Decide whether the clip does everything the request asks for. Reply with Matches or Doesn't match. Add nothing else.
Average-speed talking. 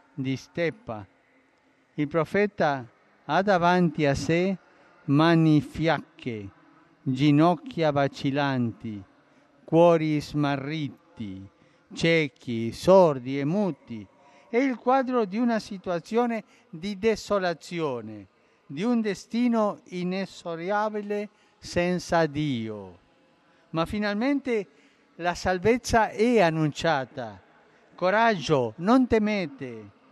Doesn't match